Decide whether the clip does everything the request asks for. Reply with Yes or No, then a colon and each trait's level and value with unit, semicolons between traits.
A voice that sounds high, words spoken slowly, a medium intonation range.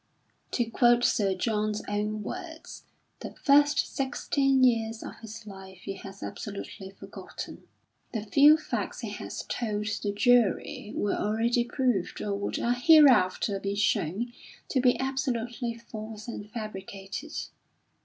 Yes: high, 225 Hz; slow, 130 wpm; average, 3.4 semitones